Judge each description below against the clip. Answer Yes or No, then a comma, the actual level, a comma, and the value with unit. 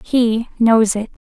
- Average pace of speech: Yes, average, 145 wpm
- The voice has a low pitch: No, high, 225 Hz